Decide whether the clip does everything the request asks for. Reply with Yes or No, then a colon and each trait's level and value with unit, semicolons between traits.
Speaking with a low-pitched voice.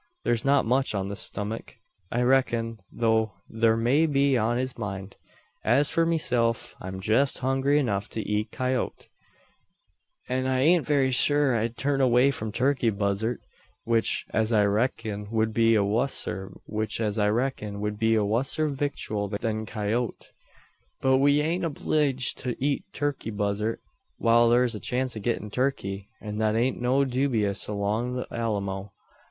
Yes: low, 115 Hz